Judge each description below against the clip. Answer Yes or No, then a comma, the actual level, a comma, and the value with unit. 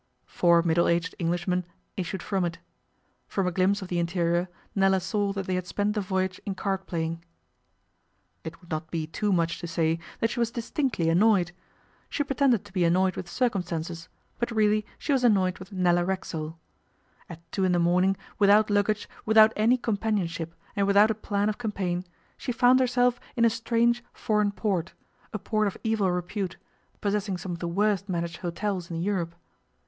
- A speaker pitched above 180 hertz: Yes, high, 190 Hz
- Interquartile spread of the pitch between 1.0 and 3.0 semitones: No, average, 3.6 semitones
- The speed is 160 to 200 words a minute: Yes, average, 180 wpm